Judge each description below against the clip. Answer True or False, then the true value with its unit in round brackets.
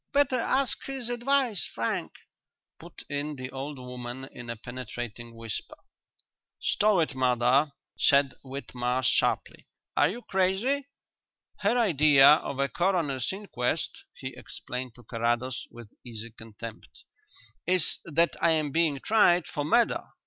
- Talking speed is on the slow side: True (130 wpm)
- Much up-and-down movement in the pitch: True (7.5 semitones)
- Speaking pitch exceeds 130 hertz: True (140 Hz)